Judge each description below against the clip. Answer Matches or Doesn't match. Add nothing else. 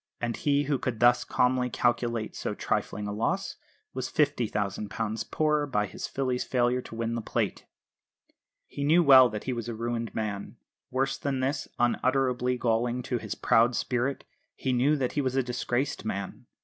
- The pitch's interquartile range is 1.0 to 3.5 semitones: Matches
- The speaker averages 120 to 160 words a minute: Doesn't match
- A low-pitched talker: Matches